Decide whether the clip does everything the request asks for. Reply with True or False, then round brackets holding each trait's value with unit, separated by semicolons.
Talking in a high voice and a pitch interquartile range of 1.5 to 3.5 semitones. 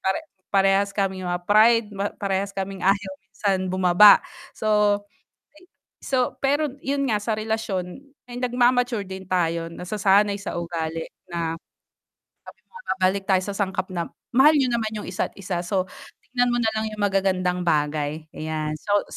True (195 Hz; 3.0 semitones)